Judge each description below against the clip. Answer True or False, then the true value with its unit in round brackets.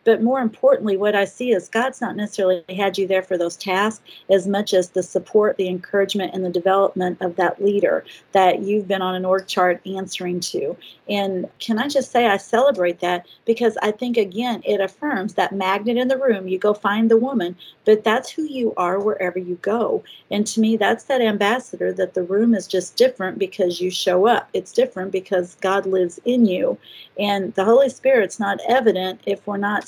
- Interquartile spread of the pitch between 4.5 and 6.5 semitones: False (3.4 semitones)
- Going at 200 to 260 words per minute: True (205 wpm)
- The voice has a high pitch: True (200 Hz)